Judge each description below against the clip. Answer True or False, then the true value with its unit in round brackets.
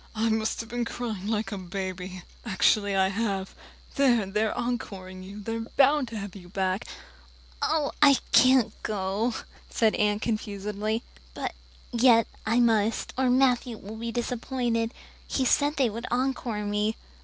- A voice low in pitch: False (220 Hz)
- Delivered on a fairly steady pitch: False (3.2 semitones)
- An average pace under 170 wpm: True (145 wpm)